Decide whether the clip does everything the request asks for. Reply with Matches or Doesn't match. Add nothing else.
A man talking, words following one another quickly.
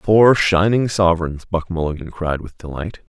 Doesn't match